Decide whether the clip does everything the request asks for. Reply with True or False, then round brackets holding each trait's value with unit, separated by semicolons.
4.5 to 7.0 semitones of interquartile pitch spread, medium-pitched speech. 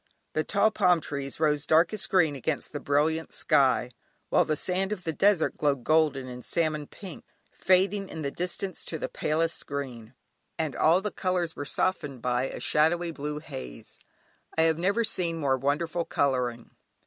False (3.8 semitones; 155 Hz)